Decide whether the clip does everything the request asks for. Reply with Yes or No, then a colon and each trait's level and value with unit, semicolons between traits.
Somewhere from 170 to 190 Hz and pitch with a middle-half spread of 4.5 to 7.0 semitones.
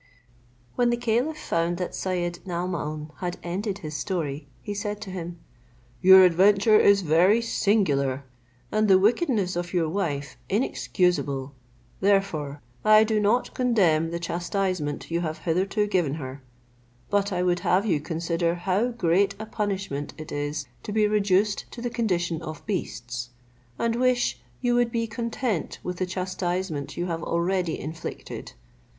No: medium, 185 Hz; average, 4.1 semitones